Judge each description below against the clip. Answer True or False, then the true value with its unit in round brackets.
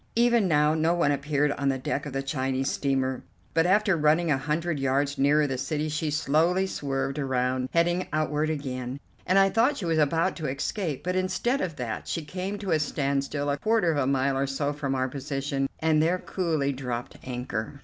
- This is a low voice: False (150 Hz)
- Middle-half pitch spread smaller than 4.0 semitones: True (3.6 semitones)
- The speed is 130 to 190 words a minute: False (200 wpm)